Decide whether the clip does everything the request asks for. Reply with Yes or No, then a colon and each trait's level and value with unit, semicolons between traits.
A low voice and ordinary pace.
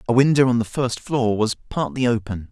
No: low, 120 Hz; fast, 215 wpm